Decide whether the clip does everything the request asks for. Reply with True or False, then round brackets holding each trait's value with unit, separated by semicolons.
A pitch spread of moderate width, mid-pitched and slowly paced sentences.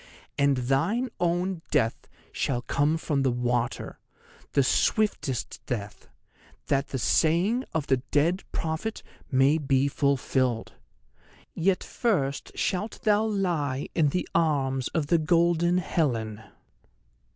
True (4.7 semitones; 145 Hz; 110 wpm)